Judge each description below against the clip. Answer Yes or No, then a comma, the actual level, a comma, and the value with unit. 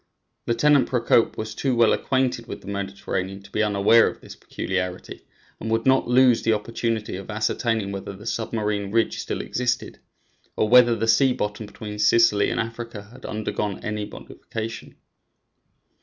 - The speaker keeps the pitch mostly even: Yes, narrow, 2.3 semitones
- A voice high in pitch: No, low, 110 Hz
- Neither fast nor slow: Yes, average, 155 wpm